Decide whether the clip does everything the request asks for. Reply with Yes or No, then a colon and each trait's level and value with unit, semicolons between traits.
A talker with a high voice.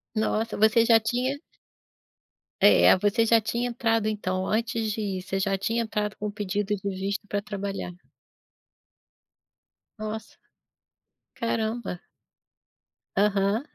Yes: high, 215 Hz